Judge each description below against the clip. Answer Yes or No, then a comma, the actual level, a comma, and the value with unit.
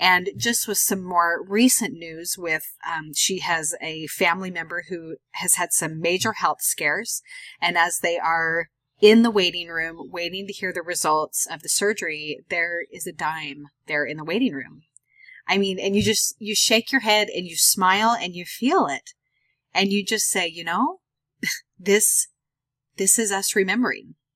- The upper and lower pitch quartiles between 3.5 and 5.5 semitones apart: Yes, average, 3.8 semitones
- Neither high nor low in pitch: Yes, medium, 180 Hz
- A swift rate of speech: No, average, 180 wpm